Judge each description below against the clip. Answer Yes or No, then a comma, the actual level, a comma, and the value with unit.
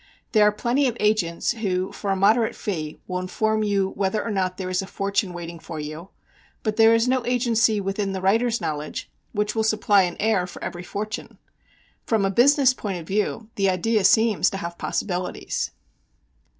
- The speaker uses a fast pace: No, average, 190 wpm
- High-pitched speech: Yes, high, 205 Hz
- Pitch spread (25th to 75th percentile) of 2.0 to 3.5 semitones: Yes, average, 3.2 semitones